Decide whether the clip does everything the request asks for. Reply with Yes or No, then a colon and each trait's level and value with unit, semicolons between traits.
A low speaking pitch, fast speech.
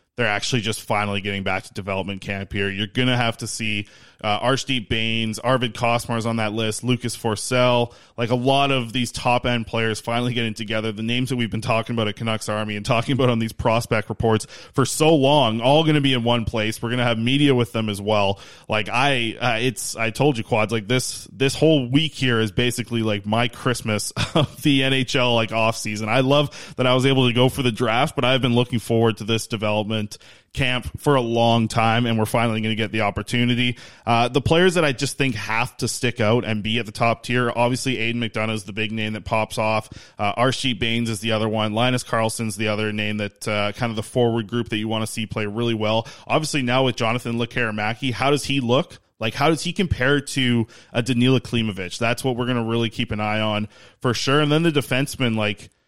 Yes: low, 115 Hz; fast, 230 wpm